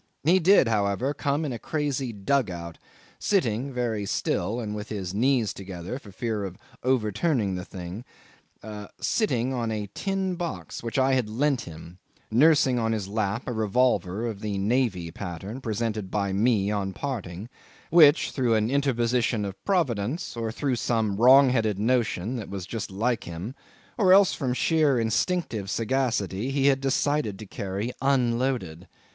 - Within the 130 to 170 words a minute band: Yes, average, 160 wpm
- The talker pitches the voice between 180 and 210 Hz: No, low, 115 Hz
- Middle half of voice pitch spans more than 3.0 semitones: Yes, average, 5.0 semitones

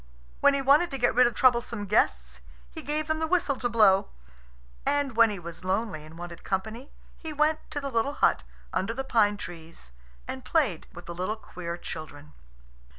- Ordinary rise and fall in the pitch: No, wide, 7.9 semitones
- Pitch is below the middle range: No, high, 225 Hz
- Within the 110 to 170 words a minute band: No, average, 190 wpm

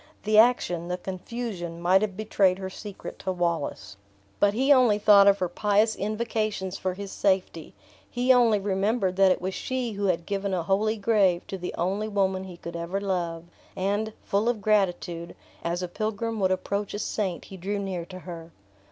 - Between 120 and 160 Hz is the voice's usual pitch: No, high, 195 Hz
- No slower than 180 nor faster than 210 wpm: Yes, average, 185 wpm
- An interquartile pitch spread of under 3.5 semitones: Yes, average, 2.8 semitones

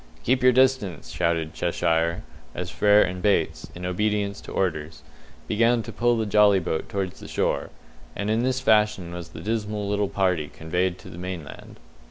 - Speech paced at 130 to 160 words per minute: No, average, 175 wpm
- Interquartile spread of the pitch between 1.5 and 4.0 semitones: Yes, average, 3.7 semitones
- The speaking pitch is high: No, low, 100 Hz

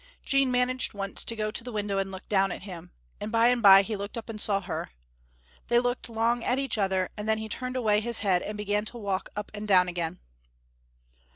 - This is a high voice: Yes, high, 210 Hz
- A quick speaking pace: Yes, fast, 230 wpm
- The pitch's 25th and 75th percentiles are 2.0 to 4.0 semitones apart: Yes, average, 3.1 semitones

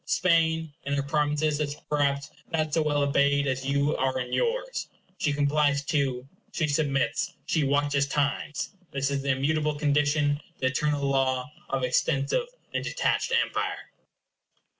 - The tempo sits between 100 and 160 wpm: Yes, average, 145 wpm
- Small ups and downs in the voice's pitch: Yes, narrow, 1.5 semitones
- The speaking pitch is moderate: Yes, medium, 145 Hz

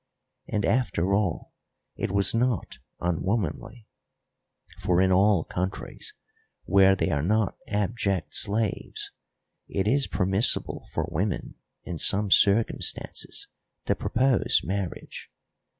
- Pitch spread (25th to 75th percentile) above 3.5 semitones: No, average, 3.0 semitones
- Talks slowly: Yes, slow, 105 wpm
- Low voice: Yes, low, 100 Hz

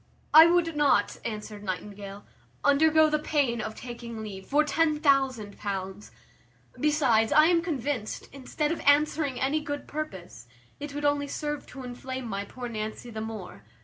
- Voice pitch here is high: Yes, very high, 260 Hz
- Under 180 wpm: Yes, average, 155 wpm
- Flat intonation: No, wide, 5.6 semitones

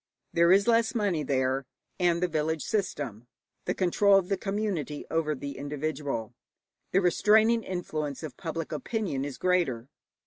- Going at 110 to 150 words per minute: Yes, average, 145 wpm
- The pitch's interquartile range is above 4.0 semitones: Yes, wide, 5.4 semitones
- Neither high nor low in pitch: Yes, medium, 165 Hz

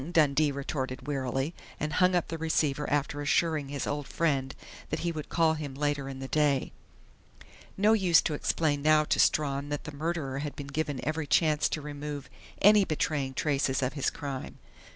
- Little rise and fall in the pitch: Yes, narrow, 2.2 semitones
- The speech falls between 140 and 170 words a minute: No, average, 185 wpm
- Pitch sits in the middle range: Yes, medium, 145 Hz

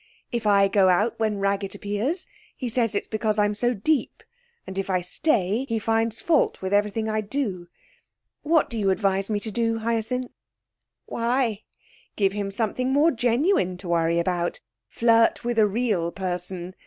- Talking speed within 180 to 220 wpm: No, average, 165 wpm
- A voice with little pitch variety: No, average, 3.3 semitones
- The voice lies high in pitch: Yes, high, 215 Hz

